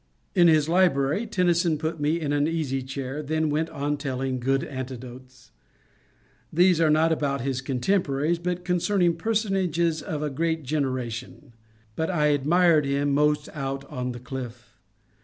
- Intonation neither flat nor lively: Yes, average, 3.7 semitones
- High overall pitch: No, medium, 150 Hz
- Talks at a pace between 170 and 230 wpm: No, average, 155 wpm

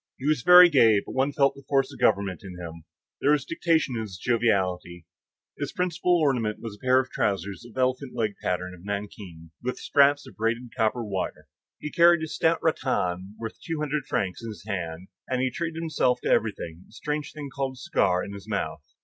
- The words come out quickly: Yes, fast, 210 wpm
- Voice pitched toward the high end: No, low, 120 Hz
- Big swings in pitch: Yes, wide, 6.5 semitones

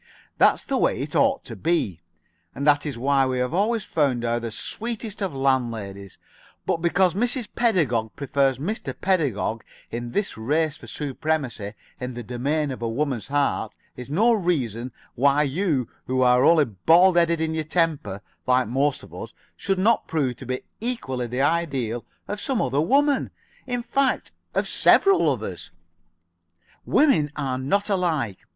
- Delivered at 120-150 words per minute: No, average, 165 wpm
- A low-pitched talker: No, medium, 145 Hz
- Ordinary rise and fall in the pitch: No, wide, 6.2 semitones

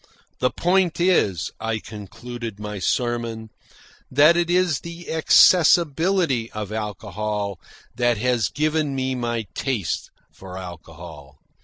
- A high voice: No, low, 120 Hz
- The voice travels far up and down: Yes, wide, 7.0 semitones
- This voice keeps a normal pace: No, slow, 115 wpm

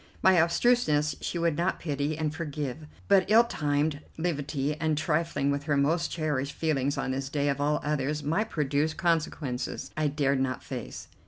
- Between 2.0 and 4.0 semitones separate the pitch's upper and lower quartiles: Yes, narrow, 2.5 semitones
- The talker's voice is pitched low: No, medium, 150 Hz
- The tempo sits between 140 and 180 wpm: Yes, average, 165 wpm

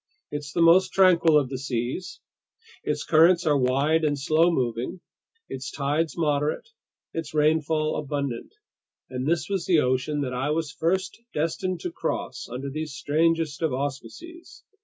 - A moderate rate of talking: Yes, average, 150 wpm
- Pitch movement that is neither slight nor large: Yes, average, 3.2 semitones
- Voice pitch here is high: No, medium, 150 Hz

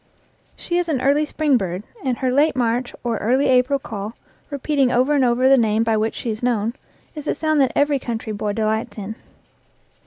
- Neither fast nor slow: No, fast, 210 wpm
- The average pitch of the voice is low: No, very high, 250 Hz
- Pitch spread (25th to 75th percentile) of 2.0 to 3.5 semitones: No, average, 4.1 semitones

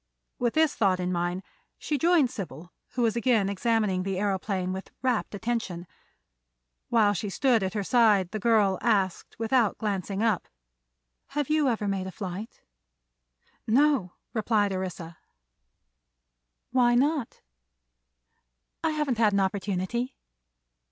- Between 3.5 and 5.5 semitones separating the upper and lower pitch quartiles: Yes, average, 4.2 semitones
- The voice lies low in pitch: No, high, 210 Hz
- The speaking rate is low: Yes, slow, 130 wpm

